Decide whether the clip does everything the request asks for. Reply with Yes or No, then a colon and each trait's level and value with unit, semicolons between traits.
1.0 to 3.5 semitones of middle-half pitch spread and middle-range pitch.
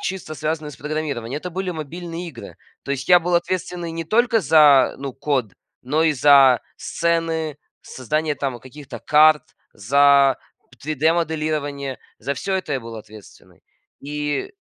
Yes: average, 3.2 semitones; medium, 150 Hz